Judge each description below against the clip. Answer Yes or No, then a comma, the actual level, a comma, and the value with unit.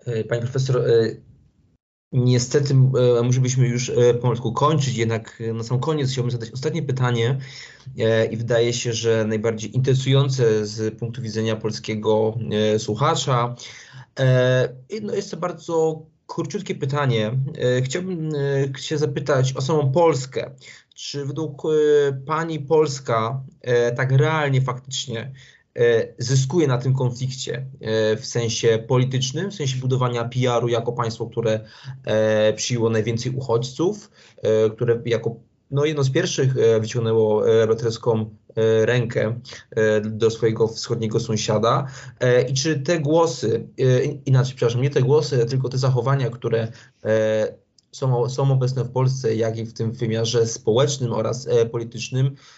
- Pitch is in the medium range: No, low, 125 Hz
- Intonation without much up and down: No, average, 3.3 semitones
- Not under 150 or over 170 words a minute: No, average, 115 wpm